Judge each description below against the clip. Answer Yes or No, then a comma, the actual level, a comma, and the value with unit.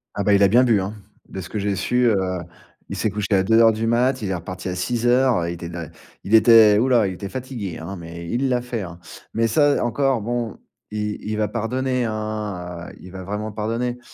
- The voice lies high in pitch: No, low, 110 Hz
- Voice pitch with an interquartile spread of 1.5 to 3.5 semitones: No, average, 4.0 semitones